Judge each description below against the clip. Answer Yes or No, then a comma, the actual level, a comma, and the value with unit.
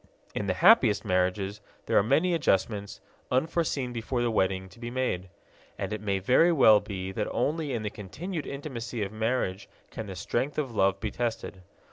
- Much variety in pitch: No, average, 4.9 semitones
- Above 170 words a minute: Yes, average, 180 wpm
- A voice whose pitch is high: No, low, 110 Hz